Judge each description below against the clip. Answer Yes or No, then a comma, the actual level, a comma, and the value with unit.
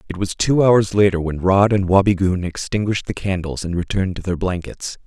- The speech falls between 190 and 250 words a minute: Yes, average, 200 wpm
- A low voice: Yes, very low, 95 Hz